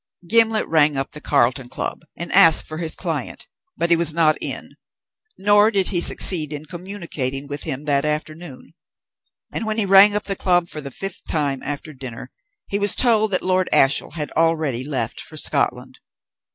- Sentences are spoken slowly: No, average, 180 wpm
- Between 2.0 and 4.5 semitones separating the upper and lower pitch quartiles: No, average, 5.0 semitones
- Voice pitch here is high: No, medium, 160 Hz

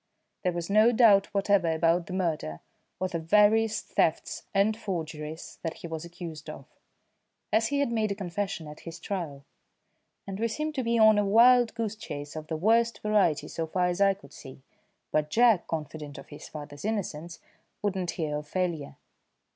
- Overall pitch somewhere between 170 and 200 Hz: Yes, medium, 185 Hz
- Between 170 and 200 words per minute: Yes, average, 185 wpm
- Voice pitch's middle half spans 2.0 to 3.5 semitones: No, average, 5.1 semitones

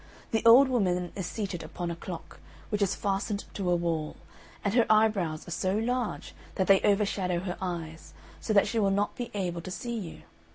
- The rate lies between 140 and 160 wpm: No, average, 200 wpm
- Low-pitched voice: No, high, 195 Hz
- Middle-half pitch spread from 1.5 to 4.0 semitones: Yes, average, 3.4 semitones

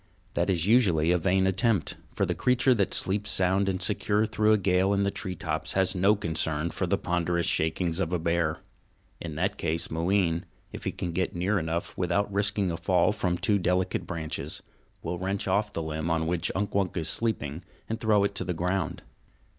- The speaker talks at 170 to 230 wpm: Yes, average, 200 wpm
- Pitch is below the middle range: Yes, very low, 90 Hz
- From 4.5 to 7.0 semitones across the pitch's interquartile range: No, average, 3.2 semitones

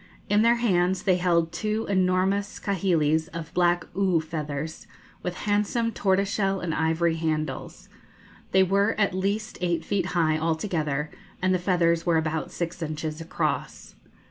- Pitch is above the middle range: No, medium, 175 Hz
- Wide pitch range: No, average, 3.3 semitones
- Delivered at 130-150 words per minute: Yes, average, 145 wpm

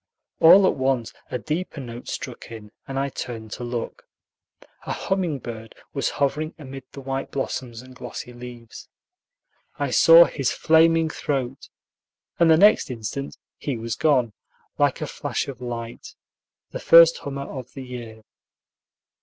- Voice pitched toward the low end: Yes, low, 130 Hz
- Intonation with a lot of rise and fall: No, average, 4.1 semitones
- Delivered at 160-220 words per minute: No, average, 150 wpm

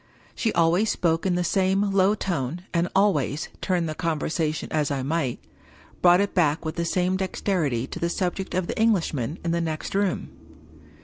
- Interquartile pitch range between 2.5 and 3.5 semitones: Yes, average, 3.2 semitones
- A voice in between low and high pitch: Yes, medium, 170 Hz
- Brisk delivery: No, average, 180 wpm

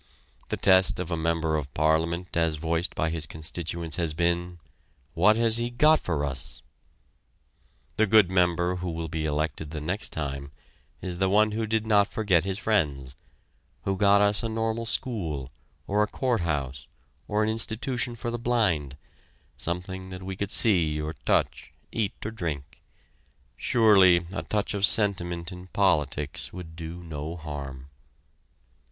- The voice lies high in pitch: No, very low, 90 Hz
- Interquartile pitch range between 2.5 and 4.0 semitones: No, average, 4.8 semitones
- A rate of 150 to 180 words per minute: Yes, average, 160 wpm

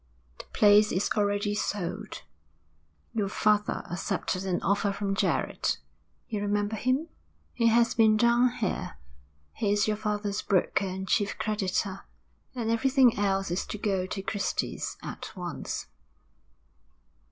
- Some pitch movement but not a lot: No, narrow, 2.0 semitones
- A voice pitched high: Yes, high, 205 Hz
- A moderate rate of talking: No, slow, 130 wpm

